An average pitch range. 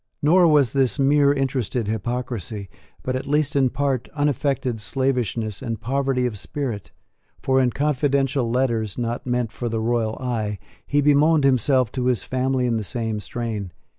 Yes: average, 3.2 semitones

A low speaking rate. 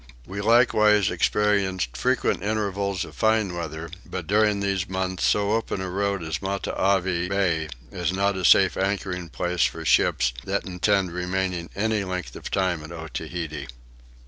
No: average, 150 wpm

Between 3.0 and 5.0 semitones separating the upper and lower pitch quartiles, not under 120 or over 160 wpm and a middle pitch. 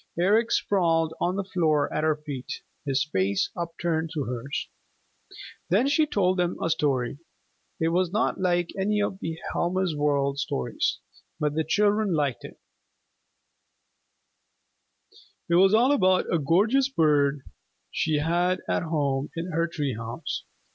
Yes: average, 4.1 semitones; average, 140 wpm; medium, 165 Hz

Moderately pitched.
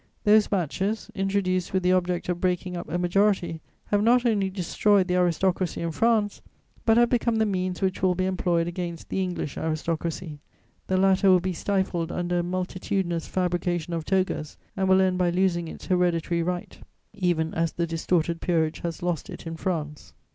Yes: medium, 180 Hz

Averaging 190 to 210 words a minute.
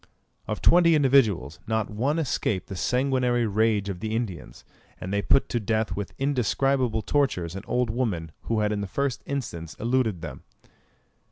No: average, 165 wpm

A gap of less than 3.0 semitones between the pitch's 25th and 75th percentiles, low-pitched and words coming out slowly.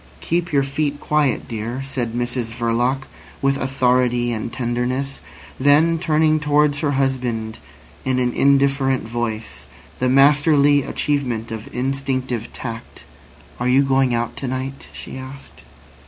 Yes: narrow, 2.6 semitones; low, 130 Hz; slow, 130 wpm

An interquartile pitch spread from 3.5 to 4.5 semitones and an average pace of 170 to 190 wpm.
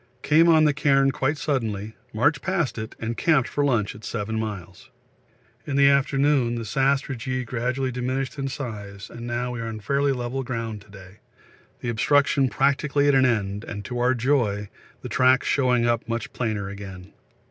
Yes: average, 3.9 semitones; average, 180 wpm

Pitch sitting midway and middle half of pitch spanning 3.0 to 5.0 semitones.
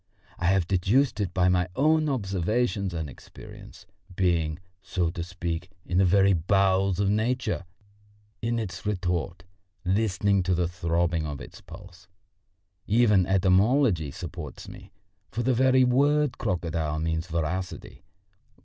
No: very low, 95 Hz; average, 3.9 semitones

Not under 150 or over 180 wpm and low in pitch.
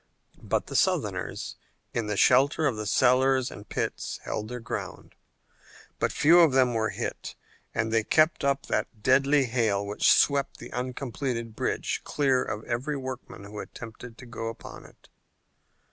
Yes: average, 160 wpm; low, 125 Hz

